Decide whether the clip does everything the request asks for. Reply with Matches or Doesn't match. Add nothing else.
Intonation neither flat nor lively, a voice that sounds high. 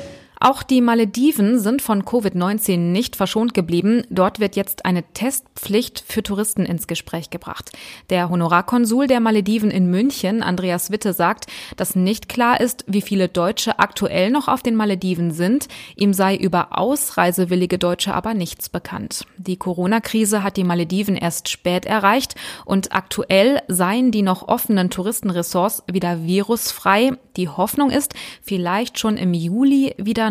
Matches